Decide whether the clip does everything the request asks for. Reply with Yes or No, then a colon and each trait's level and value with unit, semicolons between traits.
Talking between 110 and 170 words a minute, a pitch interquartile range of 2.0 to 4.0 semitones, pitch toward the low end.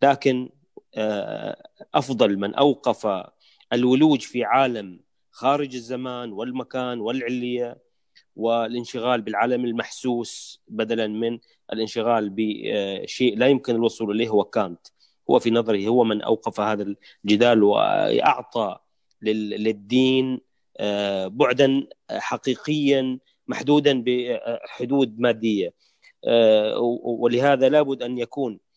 No: average, 90 wpm; average, 2.7 semitones; low, 120 Hz